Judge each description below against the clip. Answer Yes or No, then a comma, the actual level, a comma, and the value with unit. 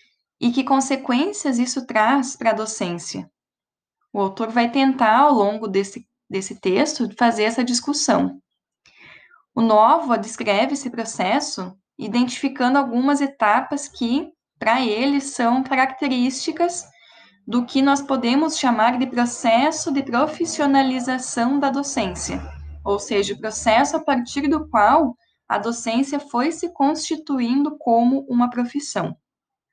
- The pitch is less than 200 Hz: No, high, 245 Hz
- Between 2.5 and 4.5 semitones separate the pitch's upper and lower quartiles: Yes, average, 3.8 semitones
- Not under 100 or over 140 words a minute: Yes, slow, 120 wpm